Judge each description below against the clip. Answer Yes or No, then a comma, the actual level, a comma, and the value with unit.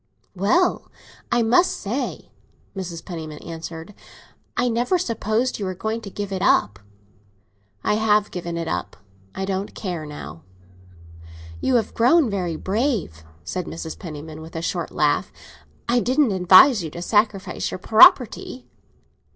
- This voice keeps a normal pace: Yes, average, 145 wpm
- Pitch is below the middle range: No, high, 195 Hz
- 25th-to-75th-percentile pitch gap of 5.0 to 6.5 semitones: Yes, wide, 5.6 semitones